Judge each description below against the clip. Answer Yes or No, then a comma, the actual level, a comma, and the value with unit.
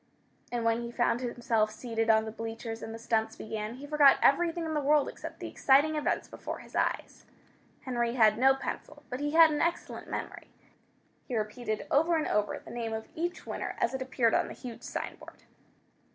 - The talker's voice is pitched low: No, high, 240 Hz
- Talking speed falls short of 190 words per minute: No, average, 195 wpm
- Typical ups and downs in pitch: Yes, average, 4.4 semitones